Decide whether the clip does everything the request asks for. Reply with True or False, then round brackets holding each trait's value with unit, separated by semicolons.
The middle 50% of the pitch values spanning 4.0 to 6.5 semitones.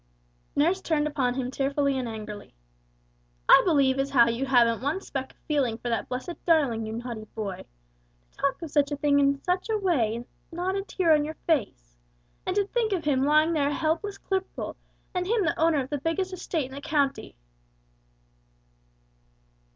True (4.9 semitones)